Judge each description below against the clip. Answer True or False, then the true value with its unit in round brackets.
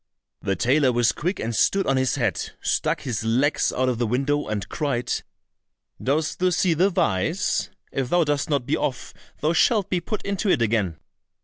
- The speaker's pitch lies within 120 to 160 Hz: True (140 Hz)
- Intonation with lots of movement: True (6.0 semitones)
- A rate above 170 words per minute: True (190 wpm)